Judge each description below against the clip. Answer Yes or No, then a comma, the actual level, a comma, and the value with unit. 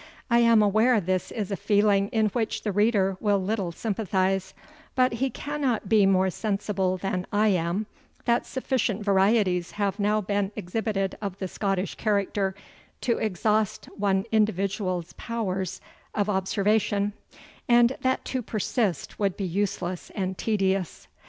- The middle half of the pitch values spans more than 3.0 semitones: No, narrow, 2.4 semitones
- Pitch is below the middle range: No, high, 205 Hz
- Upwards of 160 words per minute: No, average, 140 wpm